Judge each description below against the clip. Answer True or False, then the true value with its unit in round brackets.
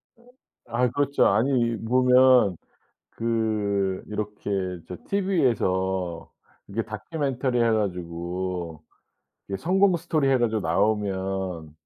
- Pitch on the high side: False (110 Hz)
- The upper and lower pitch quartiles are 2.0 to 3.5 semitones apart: False (5.2 semitones)